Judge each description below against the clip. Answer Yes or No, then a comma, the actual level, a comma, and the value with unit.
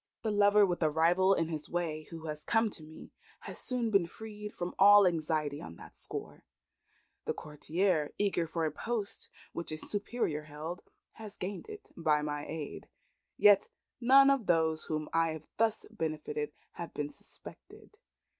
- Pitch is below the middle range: No, medium, 170 Hz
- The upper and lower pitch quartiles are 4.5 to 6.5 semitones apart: Yes, average, 5.0 semitones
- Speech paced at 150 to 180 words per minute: Yes, average, 165 wpm